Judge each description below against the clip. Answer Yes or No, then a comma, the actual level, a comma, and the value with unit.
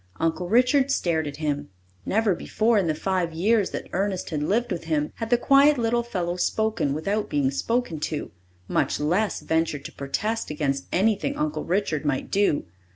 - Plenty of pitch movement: Yes, wide, 6.5 semitones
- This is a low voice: No, medium, 185 Hz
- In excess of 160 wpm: Yes, average, 175 wpm